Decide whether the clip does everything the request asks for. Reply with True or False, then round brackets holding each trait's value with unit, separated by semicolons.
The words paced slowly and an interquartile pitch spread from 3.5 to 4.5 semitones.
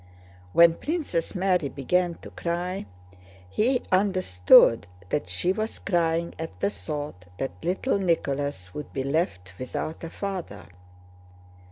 False (125 wpm; 5.3 semitones)